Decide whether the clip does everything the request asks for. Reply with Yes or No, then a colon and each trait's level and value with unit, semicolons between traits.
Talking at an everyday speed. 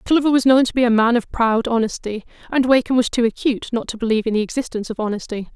No: fast, 250 wpm